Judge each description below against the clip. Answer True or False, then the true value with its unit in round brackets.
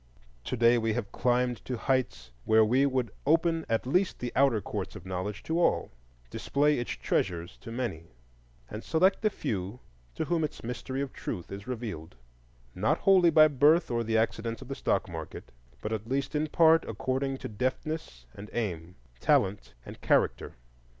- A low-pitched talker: True (120 Hz)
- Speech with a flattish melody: False (5.2 semitones)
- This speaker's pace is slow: False (175 wpm)